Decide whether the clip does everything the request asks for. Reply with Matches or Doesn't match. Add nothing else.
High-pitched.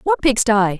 Matches